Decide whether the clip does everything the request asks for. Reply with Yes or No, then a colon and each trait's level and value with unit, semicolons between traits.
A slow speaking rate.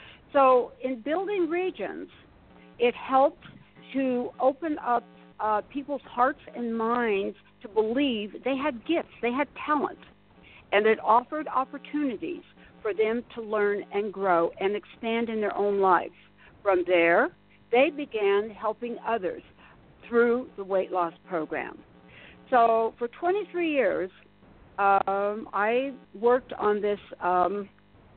Yes: slow, 125 wpm